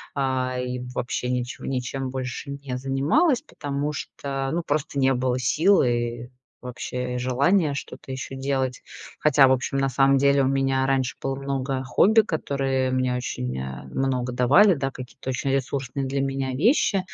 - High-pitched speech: No, low, 135 Hz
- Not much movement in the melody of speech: Yes, narrow, 1.7 semitones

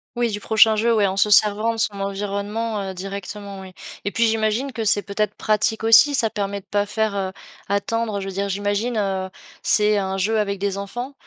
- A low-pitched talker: No, high, 205 Hz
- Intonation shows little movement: Yes, narrow, 1.9 semitones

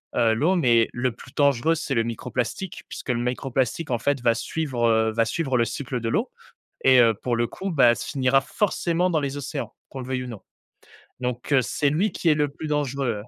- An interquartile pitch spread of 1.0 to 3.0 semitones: No, average, 3.7 semitones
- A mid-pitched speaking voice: No, low, 130 Hz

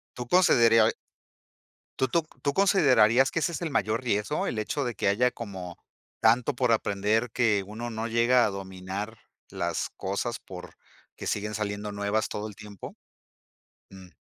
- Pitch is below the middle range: Yes, low, 110 Hz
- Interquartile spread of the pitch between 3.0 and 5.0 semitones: Yes, average, 3.4 semitones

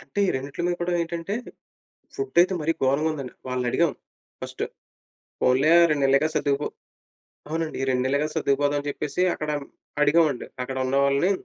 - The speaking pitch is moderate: Yes, medium, 145 Hz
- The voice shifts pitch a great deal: No, average, 3.1 semitones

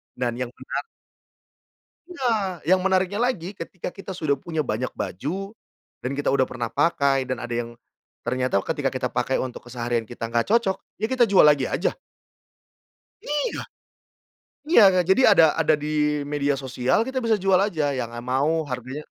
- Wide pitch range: Yes, wide, 7.1 semitones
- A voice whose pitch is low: No, medium, 145 Hz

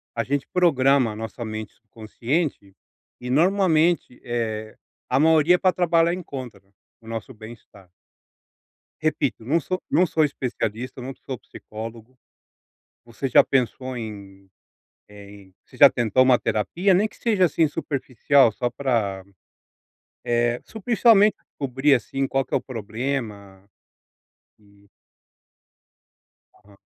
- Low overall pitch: Yes, low, 125 Hz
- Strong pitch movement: Yes, wide, 5.8 semitones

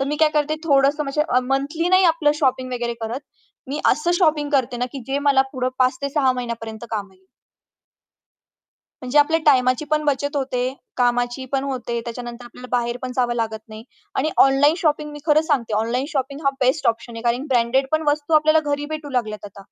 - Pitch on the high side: Yes, very high, 265 Hz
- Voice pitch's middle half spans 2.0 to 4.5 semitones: Yes, average, 3.4 semitones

